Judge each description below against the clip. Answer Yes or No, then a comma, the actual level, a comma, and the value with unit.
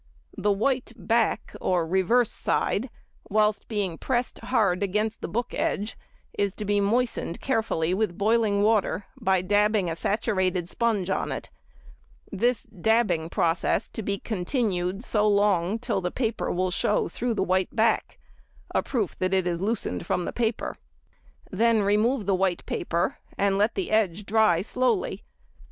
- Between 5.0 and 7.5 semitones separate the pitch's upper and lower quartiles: No, average, 3.3 semitones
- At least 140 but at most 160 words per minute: Yes, average, 150 wpm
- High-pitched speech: Yes, high, 205 Hz